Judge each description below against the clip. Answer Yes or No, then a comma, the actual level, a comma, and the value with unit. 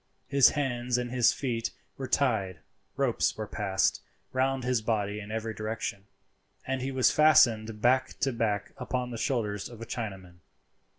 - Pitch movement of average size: Yes, average, 3.4 semitones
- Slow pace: No, average, 160 wpm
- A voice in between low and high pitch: No, low, 115 Hz